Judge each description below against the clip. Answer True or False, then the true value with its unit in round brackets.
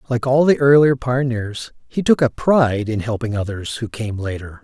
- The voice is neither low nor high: False (125 Hz)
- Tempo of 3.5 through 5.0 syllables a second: True (4.9 syllables/s)